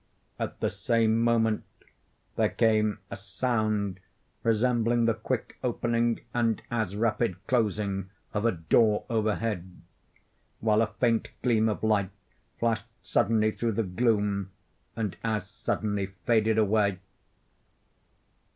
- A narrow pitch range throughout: Yes, narrow, 2.0 semitones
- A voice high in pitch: No, low, 110 Hz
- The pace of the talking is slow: Yes, slow, 115 wpm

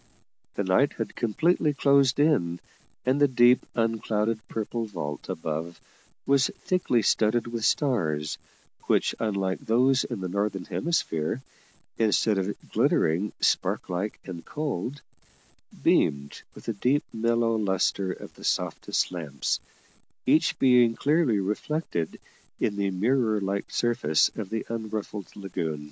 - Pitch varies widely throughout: No, average, 5.0 semitones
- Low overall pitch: Yes, low, 110 Hz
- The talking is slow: Yes, slow, 125 wpm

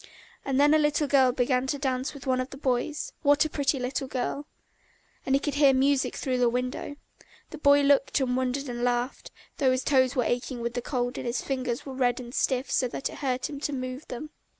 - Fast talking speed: Yes, fast, 230 wpm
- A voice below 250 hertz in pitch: No, very high, 260 Hz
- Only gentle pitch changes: Yes, narrow, 2.1 semitones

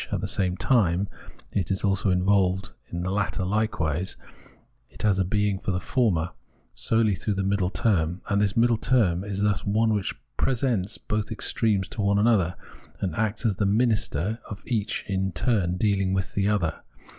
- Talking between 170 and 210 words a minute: Yes, average, 180 wpm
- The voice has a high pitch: No, low, 100 Hz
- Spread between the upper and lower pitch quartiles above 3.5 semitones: No, narrow, 2.5 semitones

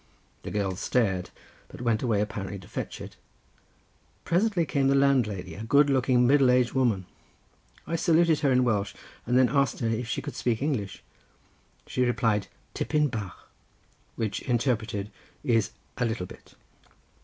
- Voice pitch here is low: Yes, low, 120 Hz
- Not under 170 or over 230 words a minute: No, average, 155 wpm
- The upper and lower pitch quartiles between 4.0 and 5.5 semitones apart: Yes, average, 4.4 semitones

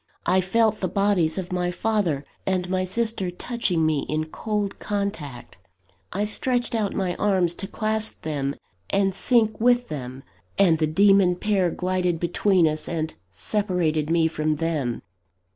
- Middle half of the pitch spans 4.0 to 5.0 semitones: Yes, average, 4.4 semitones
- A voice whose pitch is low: No, medium, 185 Hz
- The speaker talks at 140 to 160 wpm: Yes, average, 150 wpm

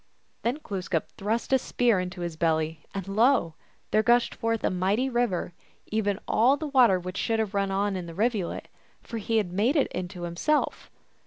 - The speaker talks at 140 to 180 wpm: No, average, 190 wpm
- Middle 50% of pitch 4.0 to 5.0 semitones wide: Yes, average, 4.5 semitones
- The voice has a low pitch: No, high, 205 Hz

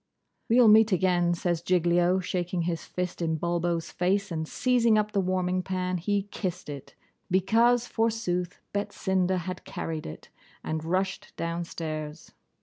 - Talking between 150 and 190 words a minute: No, average, 140 wpm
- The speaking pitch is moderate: Yes, medium, 180 Hz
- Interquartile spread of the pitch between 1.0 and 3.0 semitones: Yes, narrow, 2.5 semitones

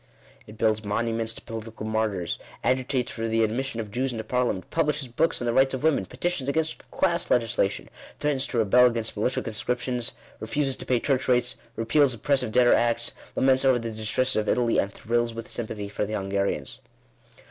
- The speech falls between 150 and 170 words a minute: No, average, 190 wpm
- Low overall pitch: Yes, low, 120 Hz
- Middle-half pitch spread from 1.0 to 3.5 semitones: Yes, average, 2.9 semitones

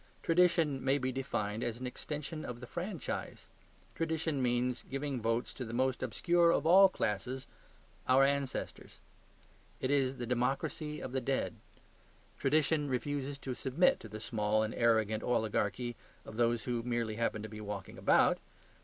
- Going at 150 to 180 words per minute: Yes, average, 155 wpm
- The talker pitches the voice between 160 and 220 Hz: No, low, 130 Hz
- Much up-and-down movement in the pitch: No, average, 3.7 semitones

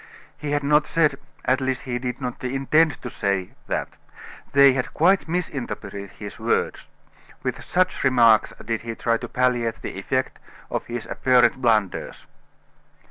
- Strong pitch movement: No, average, 3.3 semitones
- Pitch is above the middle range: No, low, 130 Hz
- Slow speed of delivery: No, average, 150 wpm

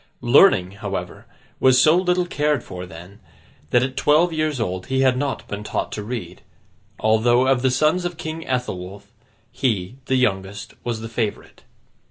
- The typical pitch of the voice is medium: No, low, 125 Hz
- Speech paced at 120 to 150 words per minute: No, average, 165 wpm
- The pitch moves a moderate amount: No, wide, 6.3 semitones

